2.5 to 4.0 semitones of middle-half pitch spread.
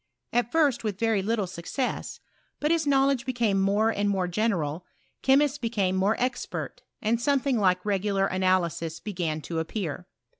No: average, 4.7 semitones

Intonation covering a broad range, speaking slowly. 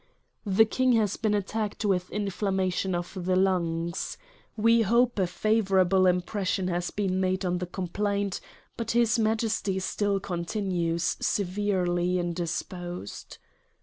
No: average, 2.7 semitones; slow, 125 wpm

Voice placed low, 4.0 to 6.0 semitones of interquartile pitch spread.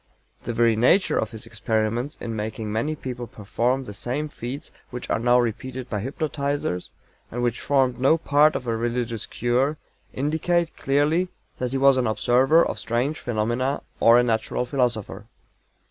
No: low, 125 Hz; average, 3.3 semitones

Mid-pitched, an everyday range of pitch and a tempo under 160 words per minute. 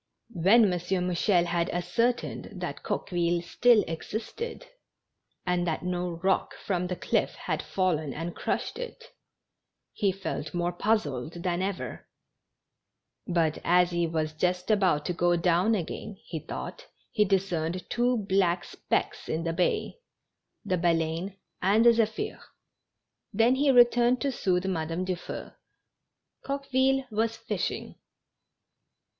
Yes: medium, 180 Hz; average, 4.2 semitones; slow, 135 wpm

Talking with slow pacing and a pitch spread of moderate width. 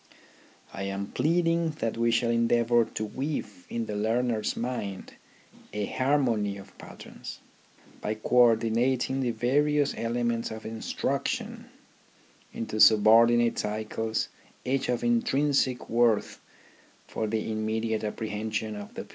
No: slow, 125 wpm; narrow, 2.2 semitones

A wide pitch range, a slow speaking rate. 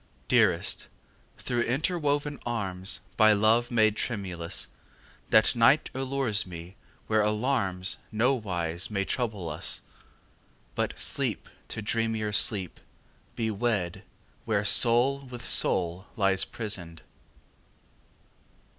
No: average, 4.1 semitones; slow, 100 wpm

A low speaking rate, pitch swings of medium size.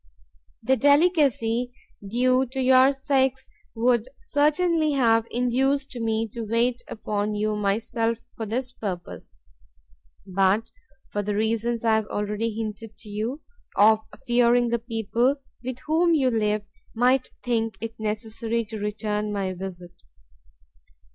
Yes: slow, 130 wpm; average, 3.2 semitones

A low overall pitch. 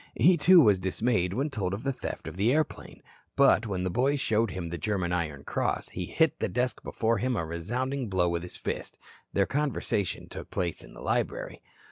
Yes: low, 105 Hz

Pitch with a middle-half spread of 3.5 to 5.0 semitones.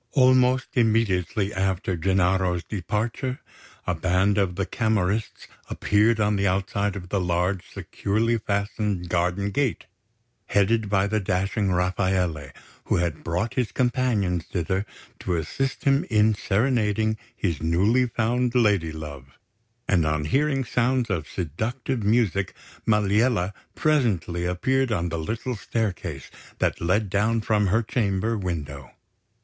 Yes: average, 4.1 semitones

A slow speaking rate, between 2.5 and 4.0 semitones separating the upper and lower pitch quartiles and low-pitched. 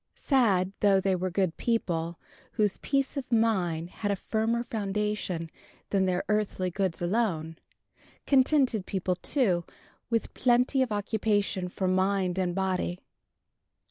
No: slow, 130 wpm; average, 3.7 semitones; high, 195 Hz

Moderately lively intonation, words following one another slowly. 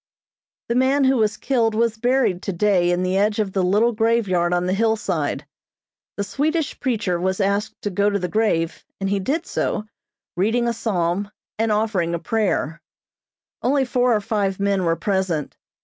No: average, 3.8 semitones; average, 175 wpm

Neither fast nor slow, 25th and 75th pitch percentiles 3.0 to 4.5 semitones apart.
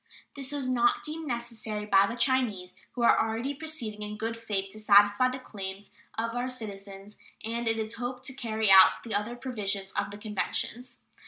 Yes: average, 185 wpm; average, 3.4 semitones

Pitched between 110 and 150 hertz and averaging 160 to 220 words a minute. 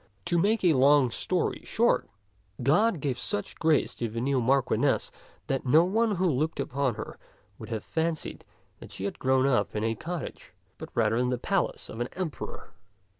Yes: medium, 140 Hz; average, 180 wpm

